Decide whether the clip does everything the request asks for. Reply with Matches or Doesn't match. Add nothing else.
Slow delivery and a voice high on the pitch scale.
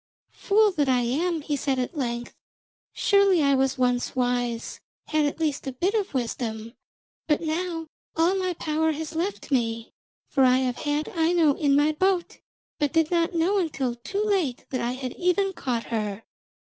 Doesn't match